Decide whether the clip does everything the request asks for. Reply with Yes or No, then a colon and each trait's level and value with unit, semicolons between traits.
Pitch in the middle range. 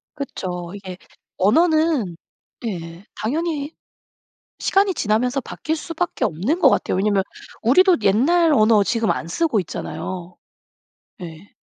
No: high, 225 Hz